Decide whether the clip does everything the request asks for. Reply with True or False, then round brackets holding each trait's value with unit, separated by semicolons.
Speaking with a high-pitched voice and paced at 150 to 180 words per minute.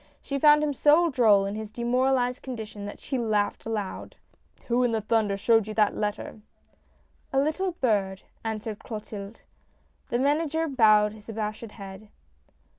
True (225 Hz; 160 wpm)